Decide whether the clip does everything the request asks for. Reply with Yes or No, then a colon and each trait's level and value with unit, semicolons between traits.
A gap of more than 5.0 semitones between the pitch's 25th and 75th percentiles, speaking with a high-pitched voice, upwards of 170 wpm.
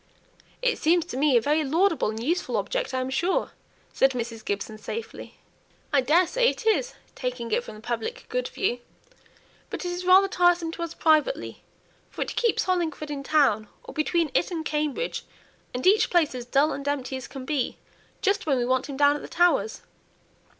Yes: wide, 5.5 semitones; very high, 300 Hz; average, 190 wpm